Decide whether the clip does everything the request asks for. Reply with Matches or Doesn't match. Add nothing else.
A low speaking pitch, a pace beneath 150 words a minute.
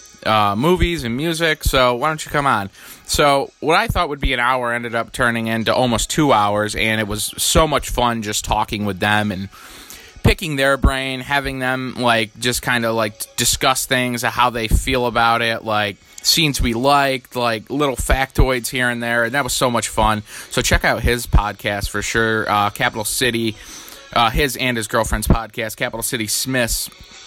Doesn't match